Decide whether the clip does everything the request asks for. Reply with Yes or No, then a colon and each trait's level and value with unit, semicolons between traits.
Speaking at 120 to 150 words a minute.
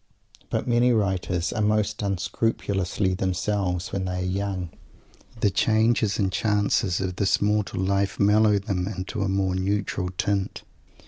Yes: average, 140 wpm